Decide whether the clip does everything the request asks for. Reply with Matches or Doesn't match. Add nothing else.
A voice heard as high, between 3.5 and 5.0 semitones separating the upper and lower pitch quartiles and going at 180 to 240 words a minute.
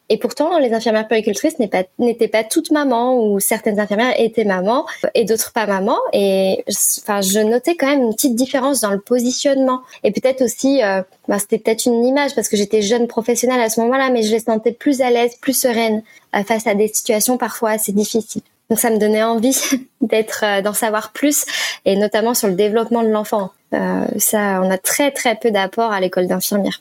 Doesn't match